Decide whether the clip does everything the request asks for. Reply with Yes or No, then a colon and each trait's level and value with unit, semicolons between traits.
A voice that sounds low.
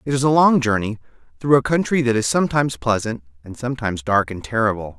Yes: low, 120 Hz